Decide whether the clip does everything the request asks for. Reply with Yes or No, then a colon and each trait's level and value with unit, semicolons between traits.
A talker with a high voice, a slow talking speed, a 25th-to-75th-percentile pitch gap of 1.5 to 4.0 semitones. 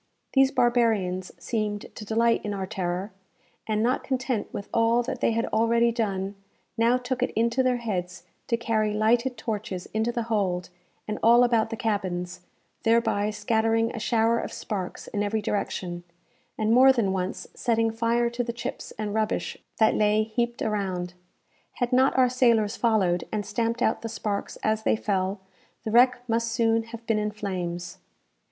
No: high, 220 Hz; average, 170 wpm; narrow, 2.4 semitones